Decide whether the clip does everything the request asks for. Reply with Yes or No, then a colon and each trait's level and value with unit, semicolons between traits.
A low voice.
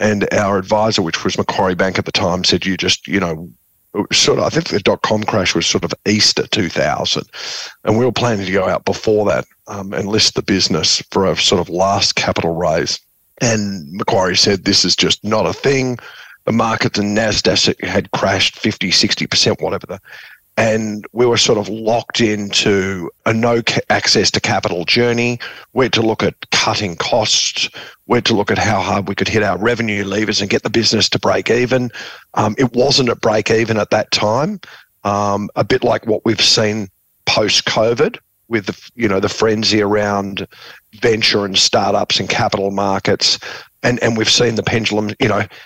Yes: low, 105 Hz